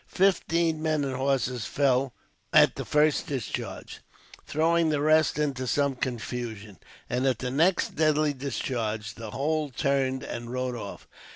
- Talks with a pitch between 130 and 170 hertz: Yes, low, 135 Hz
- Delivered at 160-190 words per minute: No, average, 145 wpm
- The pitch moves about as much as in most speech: Yes, average, 3.7 semitones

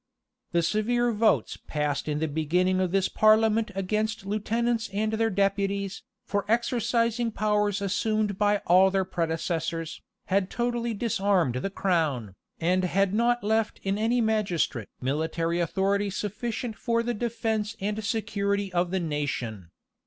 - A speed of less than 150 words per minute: Yes, average, 140 wpm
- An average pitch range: Yes, average, 3.7 semitones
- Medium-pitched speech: No, high, 200 Hz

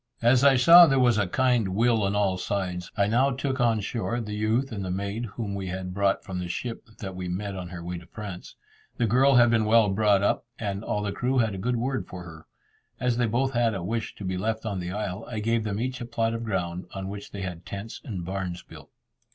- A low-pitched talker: Yes, low, 105 Hz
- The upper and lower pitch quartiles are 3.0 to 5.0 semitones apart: Yes, average, 3.8 semitones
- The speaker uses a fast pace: Yes, fast, 250 wpm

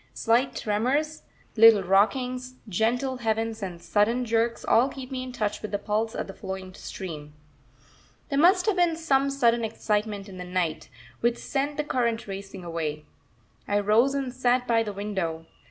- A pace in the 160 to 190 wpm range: Yes, average, 170 wpm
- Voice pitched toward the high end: Yes, high, 225 Hz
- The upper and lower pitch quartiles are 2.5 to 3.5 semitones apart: No, average, 4.4 semitones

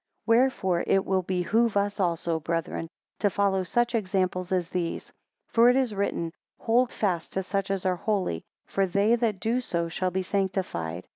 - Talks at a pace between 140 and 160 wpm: No, average, 175 wpm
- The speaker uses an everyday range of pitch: Yes, average, 3.1 semitones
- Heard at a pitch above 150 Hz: Yes, high, 190 Hz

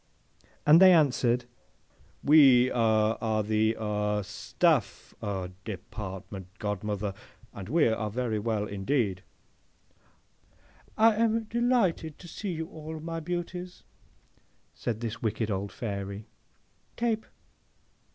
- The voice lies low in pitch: Yes, low, 115 Hz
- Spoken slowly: Yes, slow, 105 wpm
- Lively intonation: Yes, wide, 7.7 semitones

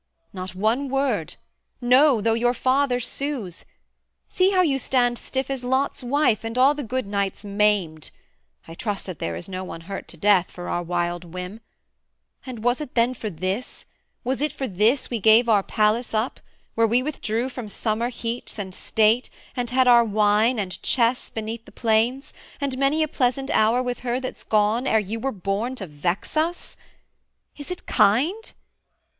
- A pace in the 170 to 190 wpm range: Yes, average, 180 wpm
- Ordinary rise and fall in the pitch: Yes, average, 4.1 semitones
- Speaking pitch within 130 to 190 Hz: No, high, 230 Hz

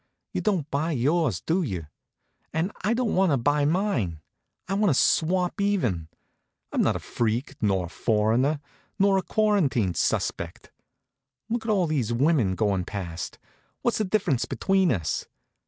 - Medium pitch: Yes, medium, 150 Hz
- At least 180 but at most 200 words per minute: No, average, 155 wpm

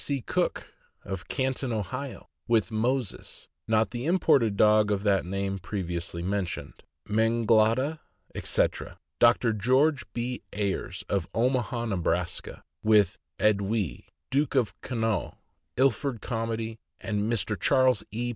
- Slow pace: Yes, slow, 110 wpm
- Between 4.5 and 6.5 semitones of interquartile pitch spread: No, average, 3.7 semitones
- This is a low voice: Yes, low, 110 Hz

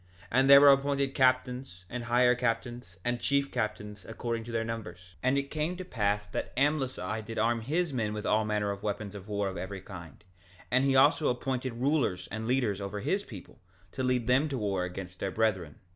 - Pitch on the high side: No, low, 115 Hz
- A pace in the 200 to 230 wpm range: Yes, fast, 205 wpm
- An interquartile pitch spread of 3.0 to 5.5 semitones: Yes, average, 4.5 semitones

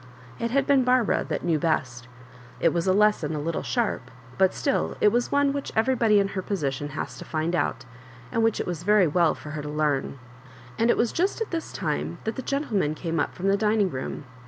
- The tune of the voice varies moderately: No, wide, 7.2 semitones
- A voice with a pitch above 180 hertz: Yes, high, 190 Hz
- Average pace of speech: No, fast, 230 wpm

